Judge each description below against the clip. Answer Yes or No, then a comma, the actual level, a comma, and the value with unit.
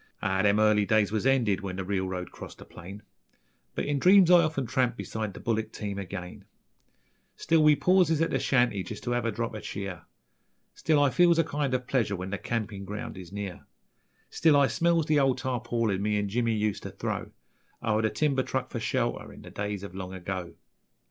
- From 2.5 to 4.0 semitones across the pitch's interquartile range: No, average, 5.3 semitones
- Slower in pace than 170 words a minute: No, fast, 205 wpm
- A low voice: Yes, low, 110 Hz